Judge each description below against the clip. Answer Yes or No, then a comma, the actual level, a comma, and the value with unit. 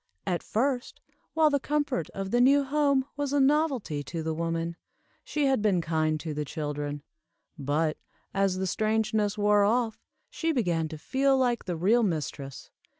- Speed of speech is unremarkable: Yes, average, 165 wpm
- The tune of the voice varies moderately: No, wide, 8.5 semitones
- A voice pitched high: Yes, high, 205 Hz